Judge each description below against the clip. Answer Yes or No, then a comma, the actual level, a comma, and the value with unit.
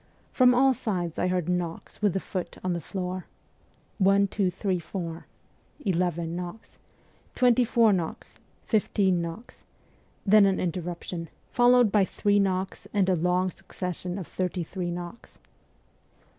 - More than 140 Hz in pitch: Yes, medium, 185 Hz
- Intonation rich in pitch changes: No, narrow, 2.6 semitones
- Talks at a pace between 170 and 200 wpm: No, average, 145 wpm